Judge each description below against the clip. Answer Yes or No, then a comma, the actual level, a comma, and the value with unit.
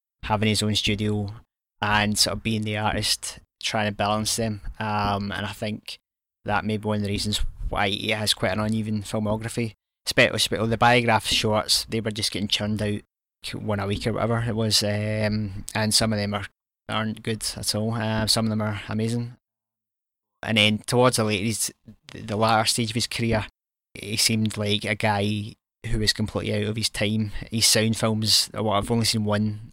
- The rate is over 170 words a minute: Yes, average, 195 wpm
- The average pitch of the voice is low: Yes, low, 110 Hz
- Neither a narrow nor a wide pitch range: No, narrow, 1.1 semitones